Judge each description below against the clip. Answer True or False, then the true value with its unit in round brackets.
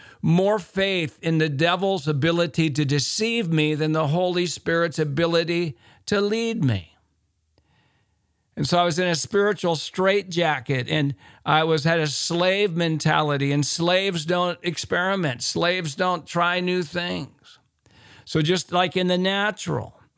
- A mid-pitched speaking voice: True (165 Hz)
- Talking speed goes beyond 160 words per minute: False (140 wpm)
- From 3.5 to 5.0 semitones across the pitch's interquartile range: True (3.9 semitones)